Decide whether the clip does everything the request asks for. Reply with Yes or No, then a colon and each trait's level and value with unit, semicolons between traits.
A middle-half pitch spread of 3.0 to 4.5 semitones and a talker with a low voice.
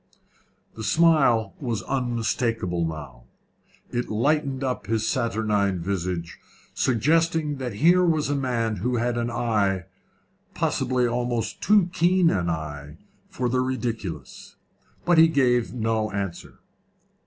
No: average, 5.2 semitones; low, 120 Hz